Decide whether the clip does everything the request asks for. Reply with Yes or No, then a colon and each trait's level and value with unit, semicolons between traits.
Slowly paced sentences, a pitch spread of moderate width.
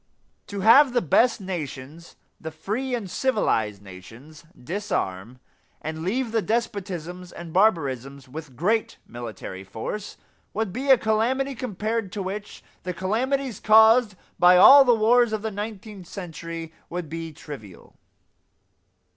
No: slow, 130 wpm; wide, 6.0 semitones